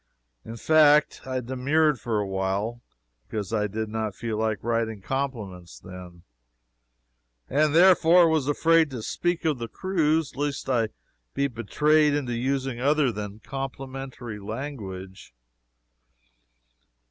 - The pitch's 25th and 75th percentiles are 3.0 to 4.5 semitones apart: No, average, 5.3 semitones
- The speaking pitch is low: Yes, low, 125 Hz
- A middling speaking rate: No, slow, 125 wpm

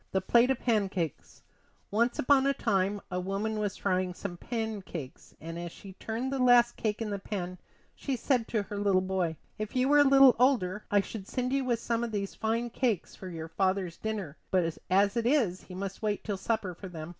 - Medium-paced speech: No, fast, 215 wpm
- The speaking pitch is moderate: No, high, 205 Hz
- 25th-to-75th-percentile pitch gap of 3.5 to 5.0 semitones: Yes, average, 4.2 semitones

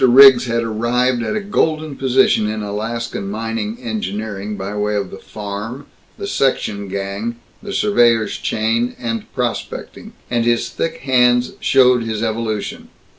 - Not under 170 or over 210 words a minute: No, average, 140 wpm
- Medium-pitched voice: No, low, 115 Hz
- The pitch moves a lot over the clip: No, average, 2.9 semitones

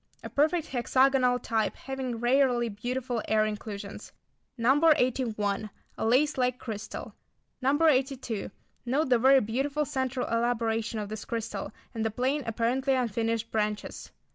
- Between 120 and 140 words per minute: Yes, slow, 135 wpm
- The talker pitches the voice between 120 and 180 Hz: No, high, 245 Hz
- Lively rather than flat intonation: No, average, 3.0 semitones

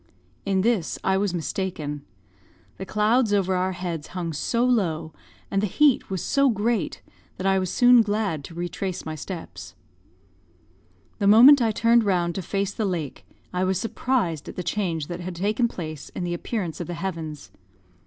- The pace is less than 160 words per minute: No, average, 175 wpm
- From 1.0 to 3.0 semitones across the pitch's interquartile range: No, average, 3.9 semitones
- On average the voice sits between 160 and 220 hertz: Yes, high, 190 Hz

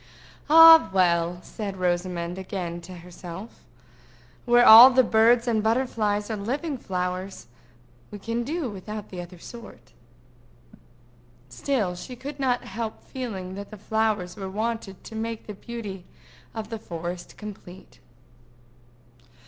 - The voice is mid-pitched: No, high, 210 Hz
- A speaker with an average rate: No, slow, 125 wpm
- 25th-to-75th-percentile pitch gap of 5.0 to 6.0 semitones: No, average, 4.4 semitones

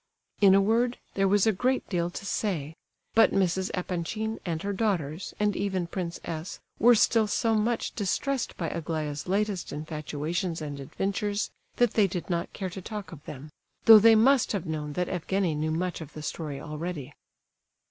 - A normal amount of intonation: Yes, average, 4.6 semitones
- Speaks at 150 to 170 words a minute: No, average, 180 wpm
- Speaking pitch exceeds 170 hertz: Yes, medium, 185 Hz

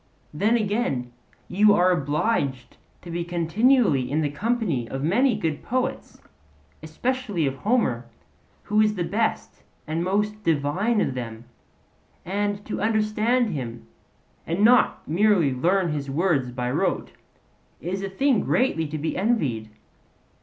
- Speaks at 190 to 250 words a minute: No, average, 140 wpm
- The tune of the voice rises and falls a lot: Yes, wide, 6.8 semitones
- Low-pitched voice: No, medium, 180 Hz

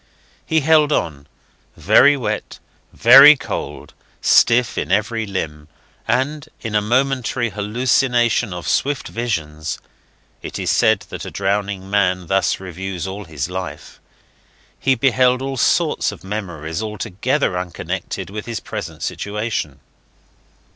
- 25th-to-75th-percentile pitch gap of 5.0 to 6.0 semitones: Yes, average, 5.3 semitones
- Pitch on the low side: Yes, low, 105 Hz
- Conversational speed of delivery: No, slow, 125 wpm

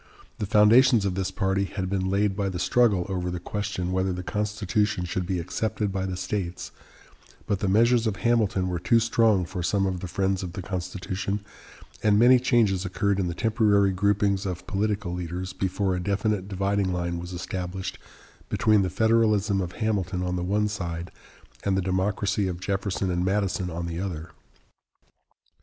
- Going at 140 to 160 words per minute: No, average, 180 wpm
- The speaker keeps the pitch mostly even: Yes, narrow, 2.3 semitones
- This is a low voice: Yes, very low, 95 Hz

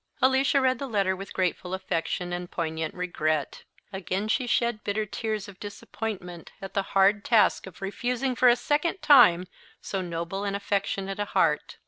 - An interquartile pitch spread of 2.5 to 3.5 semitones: No, average, 4.4 semitones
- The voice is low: No, high, 200 Hz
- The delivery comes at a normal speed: Yes, average, 170 wpm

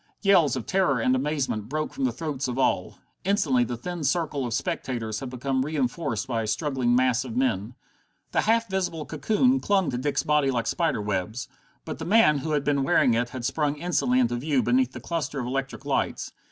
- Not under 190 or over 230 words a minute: Yes, fast, 205 wpm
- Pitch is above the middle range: No, low, 135 Hz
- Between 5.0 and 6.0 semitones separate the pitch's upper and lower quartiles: No, average, 4.3 semitones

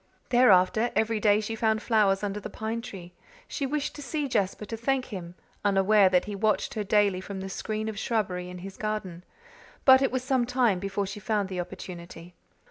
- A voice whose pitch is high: Yes, high, 210 Hz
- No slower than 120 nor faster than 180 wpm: No, average, 200 wpm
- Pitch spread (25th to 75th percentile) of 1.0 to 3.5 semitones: Yes, average, 3.0 semitones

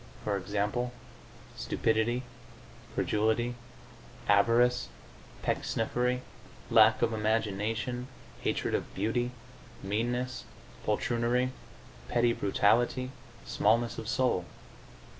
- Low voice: Yes, low, 115 Hz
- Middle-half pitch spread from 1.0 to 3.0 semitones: Yes, narrow, 2.4 semitones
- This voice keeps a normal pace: No, slow, 75 wpm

